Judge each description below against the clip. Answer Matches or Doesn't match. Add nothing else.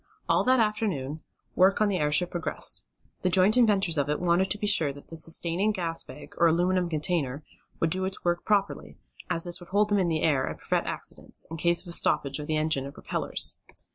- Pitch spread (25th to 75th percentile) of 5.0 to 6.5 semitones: Doesn't match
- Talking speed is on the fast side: Matches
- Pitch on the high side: Doesn't match